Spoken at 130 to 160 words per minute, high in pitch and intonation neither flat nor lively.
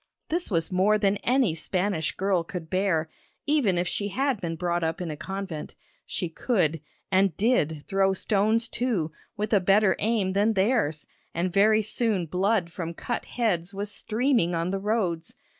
No: average, 170 wpm; high, 195 Hz; average, 4.0 semitones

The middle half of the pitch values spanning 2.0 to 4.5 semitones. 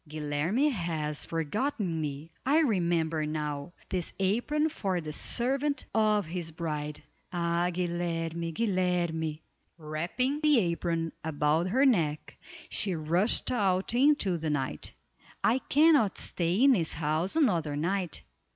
No: wide, 5.4 semitones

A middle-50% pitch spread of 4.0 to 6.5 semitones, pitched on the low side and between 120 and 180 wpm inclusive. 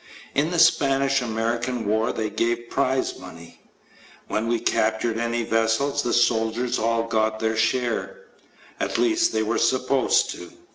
No: average, 3.2 semitones; low, 115 Hz; average, 145 wpm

